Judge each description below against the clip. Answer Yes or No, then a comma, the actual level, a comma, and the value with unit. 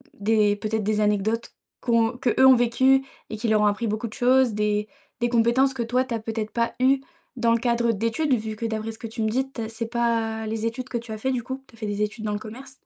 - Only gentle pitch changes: Yes, narrow, 2.0 semitones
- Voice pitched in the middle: No, high, 230 Hz